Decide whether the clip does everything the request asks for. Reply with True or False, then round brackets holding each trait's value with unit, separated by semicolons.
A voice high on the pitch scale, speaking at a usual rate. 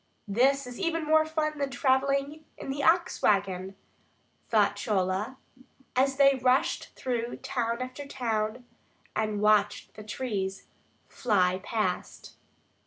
False (245 Hz; 120 wpm)